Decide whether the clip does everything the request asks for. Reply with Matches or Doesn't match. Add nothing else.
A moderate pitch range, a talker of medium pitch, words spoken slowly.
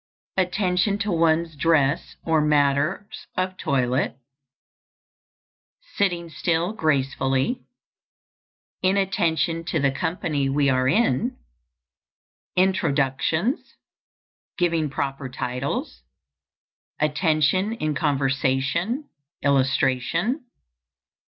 Matches